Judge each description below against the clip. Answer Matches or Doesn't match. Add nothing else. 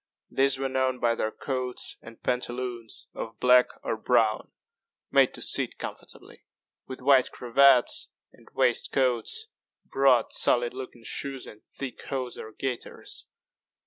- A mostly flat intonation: Matches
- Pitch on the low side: Matches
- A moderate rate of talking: Doesn't match